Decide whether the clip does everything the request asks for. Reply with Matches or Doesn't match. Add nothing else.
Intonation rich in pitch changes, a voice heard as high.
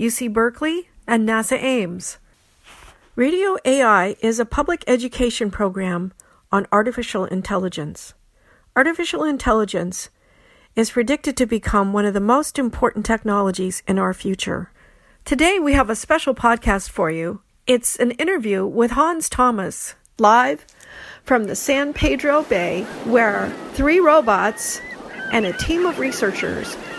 Matches